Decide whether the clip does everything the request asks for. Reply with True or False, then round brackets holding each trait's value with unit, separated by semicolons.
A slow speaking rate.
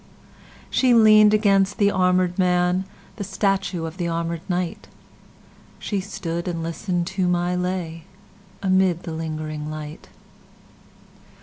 True (105 wpm)